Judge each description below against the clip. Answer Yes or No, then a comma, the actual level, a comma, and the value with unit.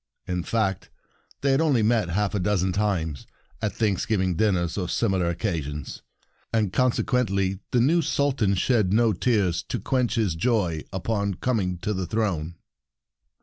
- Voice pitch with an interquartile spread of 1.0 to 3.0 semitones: No, average, 4.2 semitones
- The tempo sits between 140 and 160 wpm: Yes, average, 150 wpm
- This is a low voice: Yes, low, 100 Hz